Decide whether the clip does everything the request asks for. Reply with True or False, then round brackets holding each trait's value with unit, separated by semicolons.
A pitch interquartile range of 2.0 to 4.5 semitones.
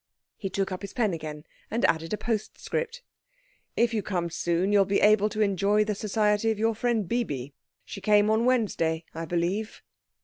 True (3.9 semitones)